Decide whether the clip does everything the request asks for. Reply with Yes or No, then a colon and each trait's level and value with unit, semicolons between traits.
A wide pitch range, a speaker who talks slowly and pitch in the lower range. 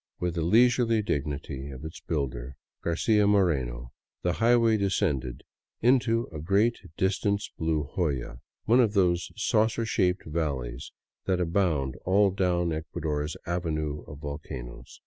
Yes: wide, 5.7 semitones; slow, 125 wpm; very low, 85 Hz